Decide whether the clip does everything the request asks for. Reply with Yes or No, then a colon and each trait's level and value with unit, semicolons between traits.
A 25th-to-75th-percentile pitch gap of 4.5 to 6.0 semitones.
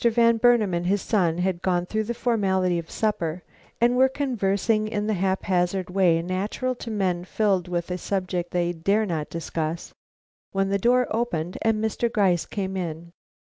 No: average, 3.7 semitones